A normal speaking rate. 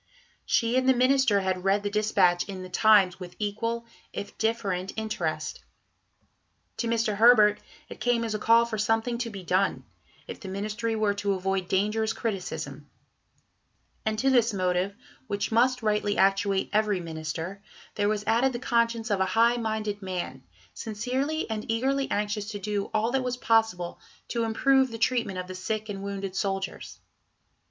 Yes: average, 165 wpm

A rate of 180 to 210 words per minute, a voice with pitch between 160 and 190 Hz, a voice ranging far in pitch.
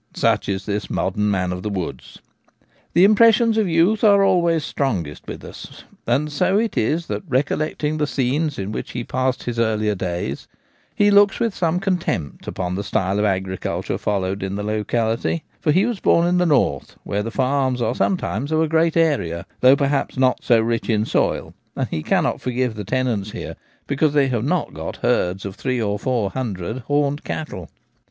No: average, 190 wpm; low, 130 Hz; wide, 7.6 semitones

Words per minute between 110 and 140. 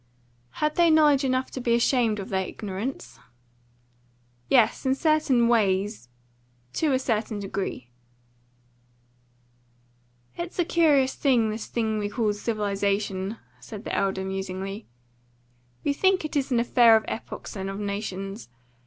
Yes: slow, 135 wpm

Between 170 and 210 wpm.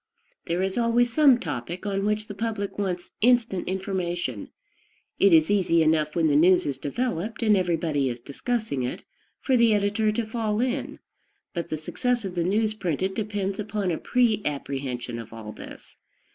Yes: average, 175 wpm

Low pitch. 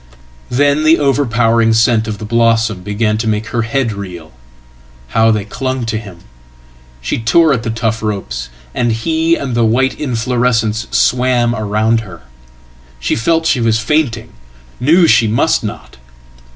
Yes: low, 115 Hz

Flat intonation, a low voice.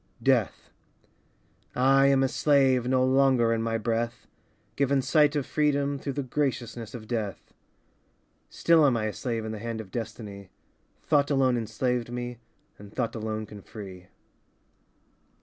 No: average, 3.5 semitones; low, 120 Hz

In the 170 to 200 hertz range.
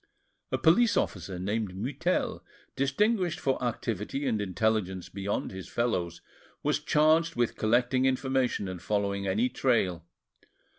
No: low, 115 Hz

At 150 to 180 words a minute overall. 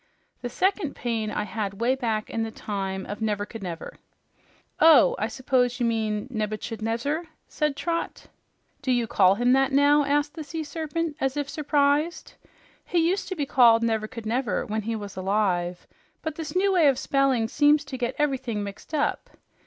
Yes: average, 170 wpm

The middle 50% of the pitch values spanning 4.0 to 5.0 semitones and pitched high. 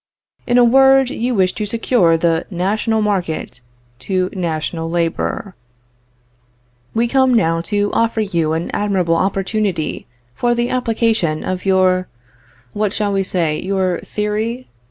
Yes: average, 4.7 semitones; high, 195 Hz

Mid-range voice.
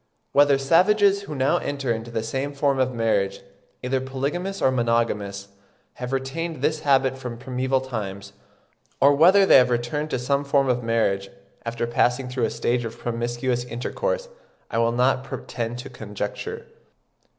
No: low, 130 Hz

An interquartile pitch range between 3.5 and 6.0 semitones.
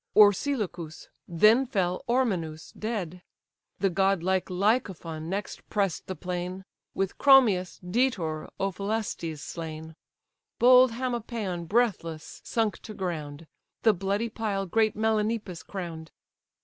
Yes: average, 4.4 semitones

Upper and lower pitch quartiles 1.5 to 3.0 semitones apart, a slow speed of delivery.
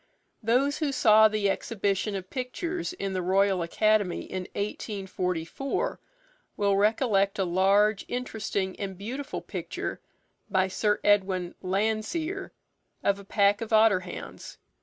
Yes: average, 2.7 semitones; slow, 125 wpm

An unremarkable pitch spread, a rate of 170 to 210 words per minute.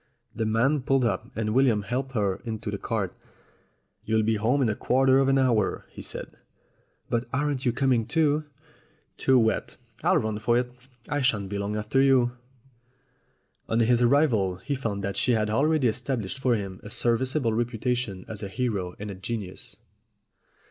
Yes: average, 3.6 semitones; average, 185 wpm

